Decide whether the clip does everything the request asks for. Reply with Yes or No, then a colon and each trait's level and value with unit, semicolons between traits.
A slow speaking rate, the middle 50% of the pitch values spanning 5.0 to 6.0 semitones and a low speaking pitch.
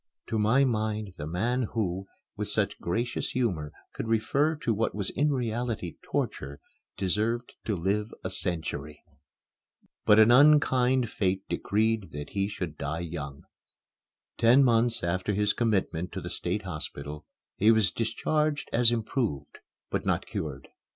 No: average, 145 wpm; average, 5.3 semitones; low, 105 Hz